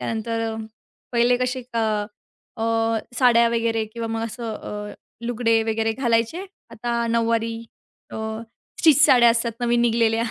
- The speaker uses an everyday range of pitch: No, narrow, 1.0 semitones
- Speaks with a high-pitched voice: Yes, high, 230 Hz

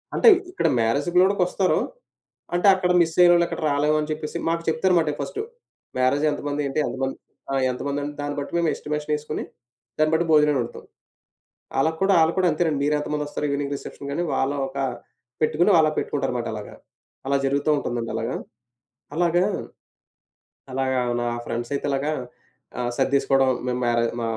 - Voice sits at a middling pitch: Yes, medium, 150 Hz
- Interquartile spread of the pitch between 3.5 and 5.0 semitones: No, average, 3.0 semitones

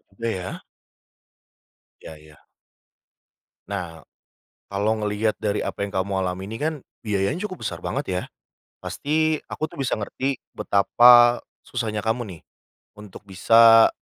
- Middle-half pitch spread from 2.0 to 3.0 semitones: No, average, 3.7 semitones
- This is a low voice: Yes, low, 105 Hz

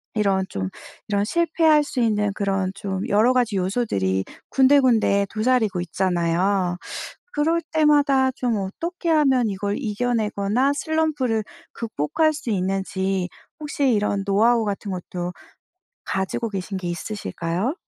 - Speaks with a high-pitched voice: Yes, high, 210 Hz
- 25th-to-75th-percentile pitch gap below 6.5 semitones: Yes, wide, 5.5 semitones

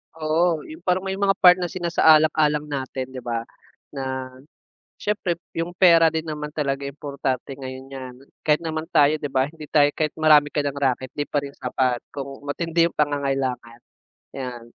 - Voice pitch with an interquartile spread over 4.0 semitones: No, average, 3.2 semitones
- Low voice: No, medium, 145 Hz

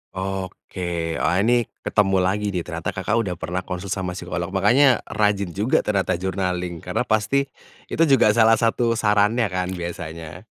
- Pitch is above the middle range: No, very low, 95 Hz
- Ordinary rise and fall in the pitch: Yes, average, 3.4 semitones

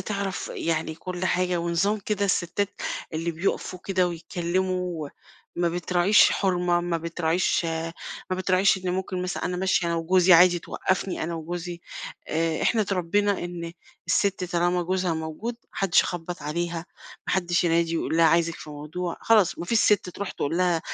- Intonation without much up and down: Yes, narrow, 1.8 semitones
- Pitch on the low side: No, medium, 175 Hz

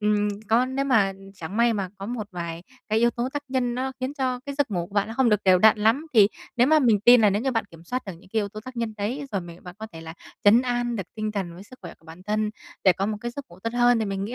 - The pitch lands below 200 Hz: No, high, 220 Hz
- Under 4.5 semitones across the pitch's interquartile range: Yes, average, 3.9 semitones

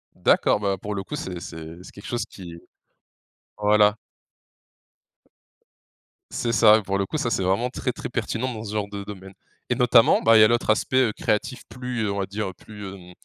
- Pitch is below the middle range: Yes, low, 105 Hz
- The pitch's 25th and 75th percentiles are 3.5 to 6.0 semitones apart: No, average, 2.8 semitones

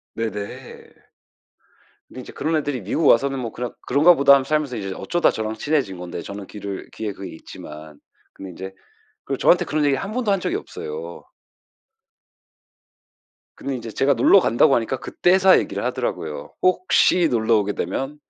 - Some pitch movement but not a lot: No, wide, 7.3 semitones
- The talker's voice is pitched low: Yes, low, 130 Hz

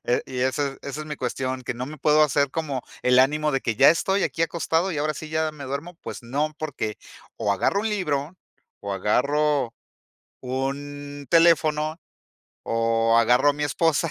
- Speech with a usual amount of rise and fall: Yes, average, 3.1 semitones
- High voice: No, medium, 145 Hz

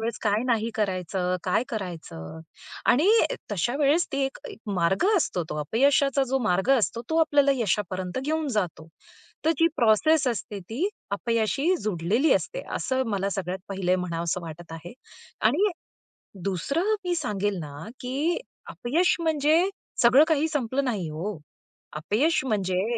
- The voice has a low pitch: No, high, 220 Hz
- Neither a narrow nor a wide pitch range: No, wide, 7.4 semitones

